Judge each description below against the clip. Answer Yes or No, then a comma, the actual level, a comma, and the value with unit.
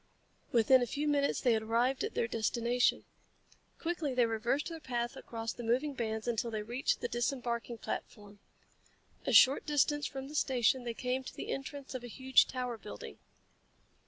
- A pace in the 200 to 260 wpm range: No, average, 175 wpm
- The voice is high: Yes, high, 245 Hz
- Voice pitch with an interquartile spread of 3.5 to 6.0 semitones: No, average, 2.7 semitones